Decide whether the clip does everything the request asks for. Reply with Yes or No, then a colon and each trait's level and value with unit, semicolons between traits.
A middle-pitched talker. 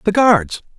No: high, 210 Hz